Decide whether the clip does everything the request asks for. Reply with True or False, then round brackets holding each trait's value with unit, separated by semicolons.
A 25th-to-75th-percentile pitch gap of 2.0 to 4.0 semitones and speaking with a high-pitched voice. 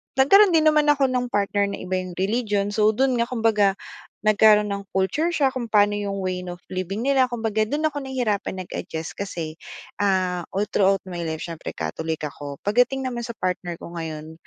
False (5.1 semitones; 205 Hz)